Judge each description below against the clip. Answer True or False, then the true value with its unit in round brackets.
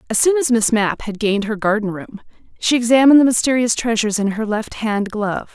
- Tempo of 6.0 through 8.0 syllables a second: True (6.1 syllables/s)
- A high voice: True (225 Hz)